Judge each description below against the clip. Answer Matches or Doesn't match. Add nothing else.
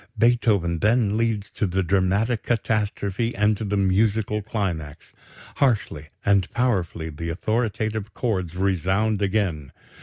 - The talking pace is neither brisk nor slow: Doesn't match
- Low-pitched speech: Matches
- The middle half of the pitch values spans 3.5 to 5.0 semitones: Doesn't match